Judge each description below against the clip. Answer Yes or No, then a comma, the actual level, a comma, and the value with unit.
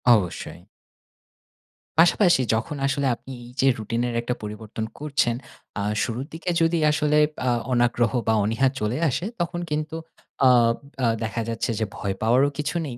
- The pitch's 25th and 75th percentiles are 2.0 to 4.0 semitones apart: No, average, 4.9 semitones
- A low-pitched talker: Yes, low, 120 Hz